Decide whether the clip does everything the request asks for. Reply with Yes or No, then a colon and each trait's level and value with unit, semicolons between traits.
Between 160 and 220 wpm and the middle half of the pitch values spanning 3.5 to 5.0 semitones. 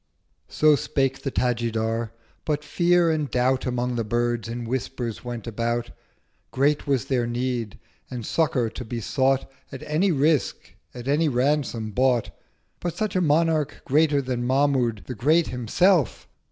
No: average, 145 wpm; average, 3.9 semitones